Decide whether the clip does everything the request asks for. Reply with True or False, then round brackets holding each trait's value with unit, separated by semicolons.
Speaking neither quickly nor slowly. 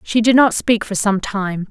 False (245 wpm)